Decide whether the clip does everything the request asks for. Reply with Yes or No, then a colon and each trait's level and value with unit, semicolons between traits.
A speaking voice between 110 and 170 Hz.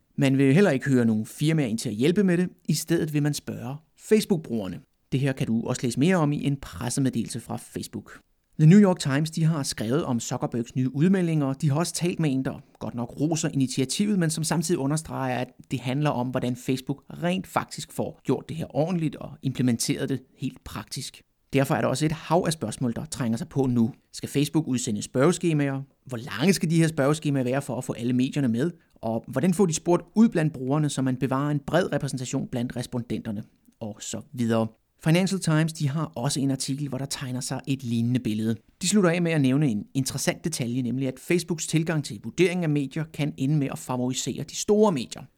Yes: medium, 140 Hz